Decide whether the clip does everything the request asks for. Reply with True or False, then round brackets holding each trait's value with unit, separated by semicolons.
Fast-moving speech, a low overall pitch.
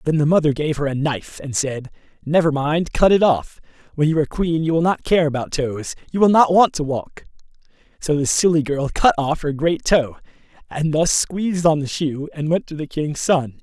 False (225 wpm; 155 Hz)